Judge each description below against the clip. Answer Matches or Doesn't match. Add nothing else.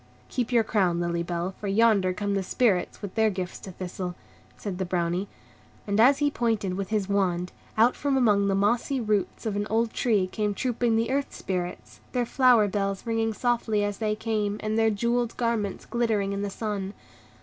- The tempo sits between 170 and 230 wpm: Matches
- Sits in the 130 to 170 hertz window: Doesn't match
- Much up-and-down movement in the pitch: Doesn't match